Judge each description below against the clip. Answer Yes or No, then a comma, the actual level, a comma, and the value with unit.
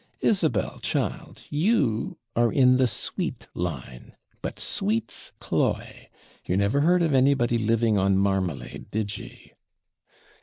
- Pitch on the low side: Yes, low, 115 Hz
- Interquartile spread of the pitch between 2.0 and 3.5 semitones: No, average, 5.0 semitones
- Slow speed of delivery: Yes, slow, 120 wpm